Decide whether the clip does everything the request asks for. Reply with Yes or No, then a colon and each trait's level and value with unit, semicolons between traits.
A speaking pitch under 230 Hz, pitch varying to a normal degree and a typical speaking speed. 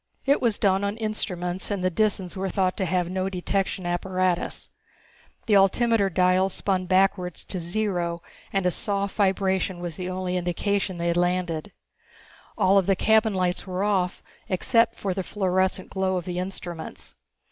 No: medium, 185 Hz; narrow, 1.7 semitones; average, 165 wpm